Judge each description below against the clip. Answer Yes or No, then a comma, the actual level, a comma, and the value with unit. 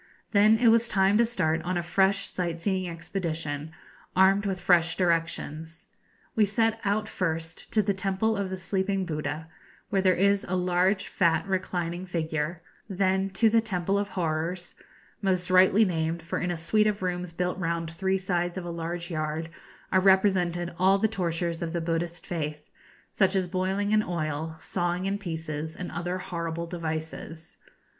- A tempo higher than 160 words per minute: Yes, average, 170 wpm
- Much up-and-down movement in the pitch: No, average, 2.7 semitones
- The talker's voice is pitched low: No, medium, 180 Hz